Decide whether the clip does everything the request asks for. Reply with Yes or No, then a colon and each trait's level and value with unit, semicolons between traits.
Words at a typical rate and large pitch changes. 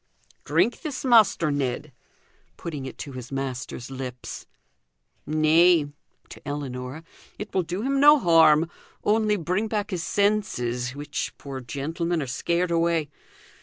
No: slow, 130 wpm; wide, 5.9 semitones